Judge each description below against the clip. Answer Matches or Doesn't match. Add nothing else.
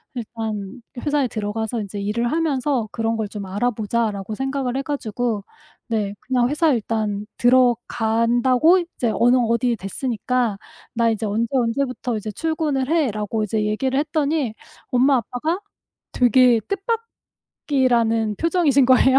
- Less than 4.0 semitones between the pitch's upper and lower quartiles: Matches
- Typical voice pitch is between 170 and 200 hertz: Doesn't match